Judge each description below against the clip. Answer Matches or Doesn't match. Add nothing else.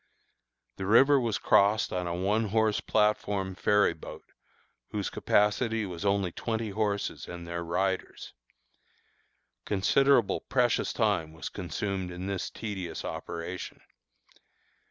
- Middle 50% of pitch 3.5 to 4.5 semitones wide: Doesn't match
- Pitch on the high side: Doesn't match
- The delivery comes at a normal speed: Doesn't match